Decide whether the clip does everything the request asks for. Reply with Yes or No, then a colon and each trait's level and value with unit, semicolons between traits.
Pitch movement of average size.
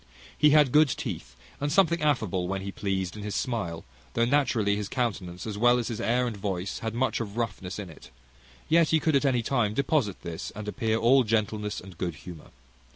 Yes: average, 4.9 semitones